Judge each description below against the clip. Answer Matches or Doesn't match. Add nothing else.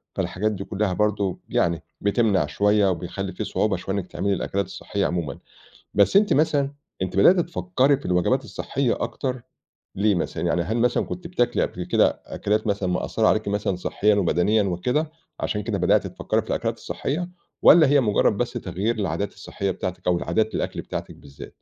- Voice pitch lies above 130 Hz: Doesn't match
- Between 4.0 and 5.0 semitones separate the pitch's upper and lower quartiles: Matches